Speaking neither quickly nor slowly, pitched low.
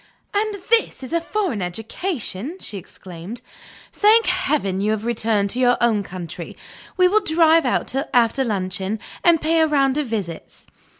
No: average, 160 wpm; high, 245 Hz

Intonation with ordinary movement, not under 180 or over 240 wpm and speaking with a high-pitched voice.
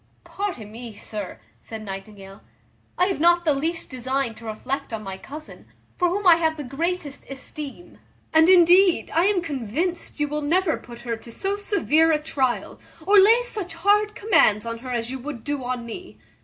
No: wide, 7.0 semitones; average, 185 wpm; very high, 295 Hz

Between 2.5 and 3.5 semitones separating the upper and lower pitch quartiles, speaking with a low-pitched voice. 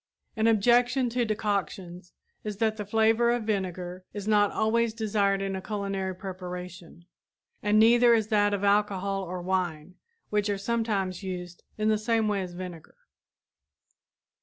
No: average, 2.9 semitones; high, 205 Hz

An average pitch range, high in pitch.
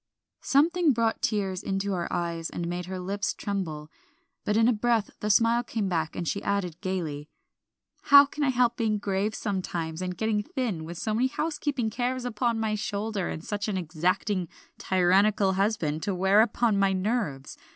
Yes: average, 4.0 semitones; high, 200 Hz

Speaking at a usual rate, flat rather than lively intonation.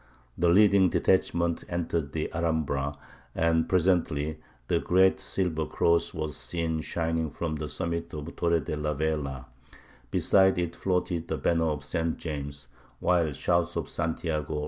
Yes: average, 145 wpm; narrow, 2.1 semitones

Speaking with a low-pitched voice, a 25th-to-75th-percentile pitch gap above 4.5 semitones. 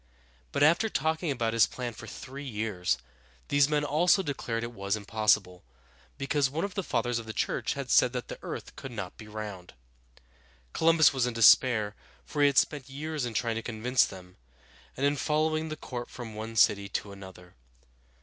Yes: low, 120 Hz; average, 5.2 semitones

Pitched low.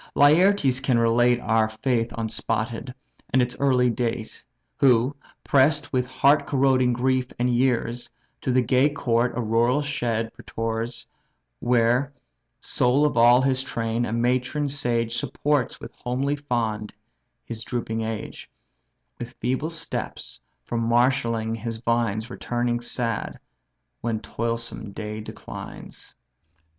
Yes: low, 120 Hz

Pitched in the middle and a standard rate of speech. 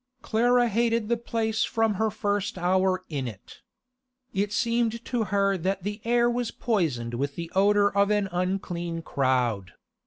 No: high, 200 Hz; average, 155 wpm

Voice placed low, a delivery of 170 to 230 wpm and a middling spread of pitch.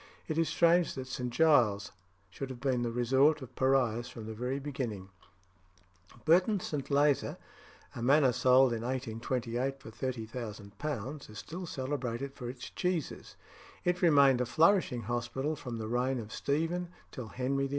No: low, 130 Hz; average, 155 wpm; average, 3.4 semitones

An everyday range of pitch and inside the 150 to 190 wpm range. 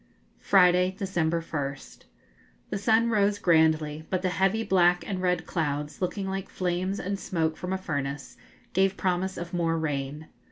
Yes: average, 3.2 semitones; average, 155 wpm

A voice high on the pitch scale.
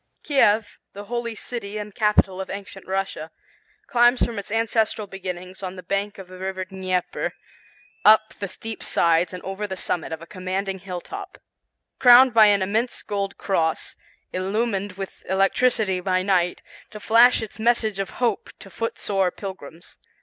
Yes: high, 195 Hz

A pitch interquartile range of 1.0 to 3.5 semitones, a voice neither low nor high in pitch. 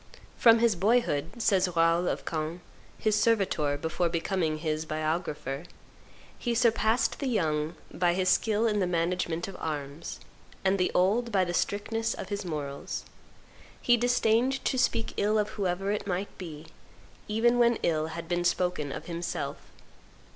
No: average, 5.2 semitones; medium, 180 Hz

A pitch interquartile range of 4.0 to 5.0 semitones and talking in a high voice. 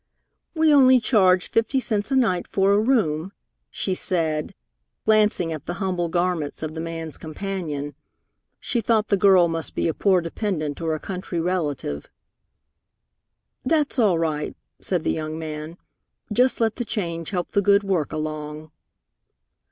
No: average, 4.7 semitones; medium, 180 Hz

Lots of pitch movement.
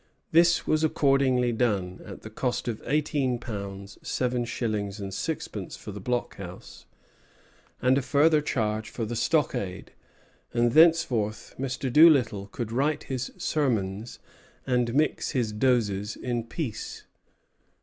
No: average, 4.4 semitones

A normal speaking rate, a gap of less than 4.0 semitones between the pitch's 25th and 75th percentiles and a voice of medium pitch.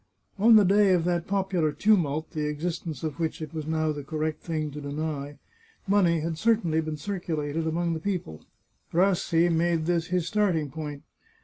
Yes: average, 175 wpm; average, 2.7 semitones; medium, 165 Hz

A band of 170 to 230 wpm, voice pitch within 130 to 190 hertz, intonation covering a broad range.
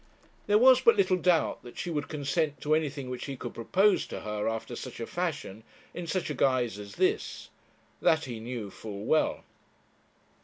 Yes: average, 185 wpm; medium, 140 Hz; wide, 6.9 semitones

